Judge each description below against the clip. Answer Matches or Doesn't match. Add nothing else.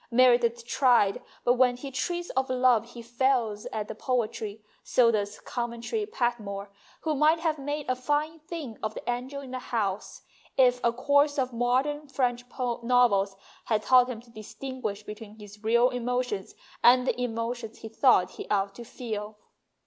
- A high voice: Matches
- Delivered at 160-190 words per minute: Matches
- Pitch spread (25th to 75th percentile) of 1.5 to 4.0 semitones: Matches